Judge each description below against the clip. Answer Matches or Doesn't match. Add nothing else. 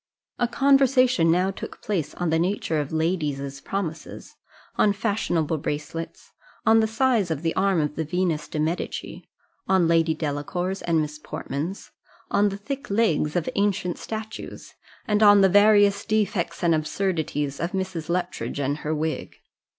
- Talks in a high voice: Doesn't match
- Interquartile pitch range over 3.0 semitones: Matches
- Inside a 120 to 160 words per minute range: Matches